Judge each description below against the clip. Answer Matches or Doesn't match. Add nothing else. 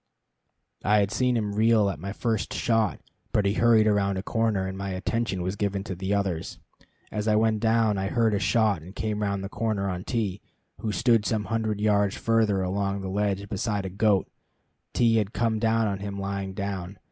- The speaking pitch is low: Matches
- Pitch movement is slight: Matches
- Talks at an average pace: Matches